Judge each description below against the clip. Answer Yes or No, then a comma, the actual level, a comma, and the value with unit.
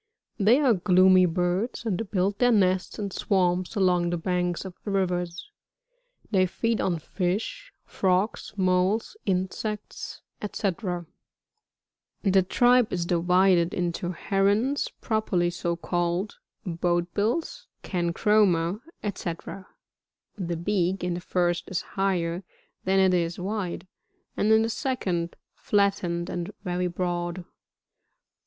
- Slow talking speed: Yes, slow, 120 wpm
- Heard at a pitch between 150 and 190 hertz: Yes, medium, 185 Hz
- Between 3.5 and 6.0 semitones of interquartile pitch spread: No, average, 2.8 semitones